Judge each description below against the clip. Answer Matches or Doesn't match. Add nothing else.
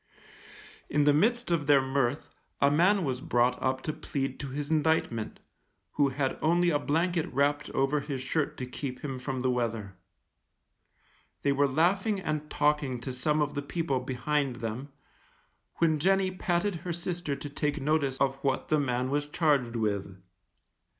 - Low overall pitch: Doesn't match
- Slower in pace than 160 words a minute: Doesn't match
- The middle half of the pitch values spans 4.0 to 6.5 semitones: Doesn't match